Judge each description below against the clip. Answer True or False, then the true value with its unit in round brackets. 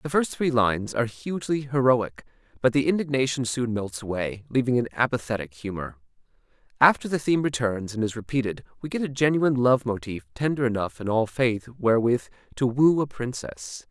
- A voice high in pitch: False (125 Hz)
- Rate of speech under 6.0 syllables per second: True (5.6 syllables/s)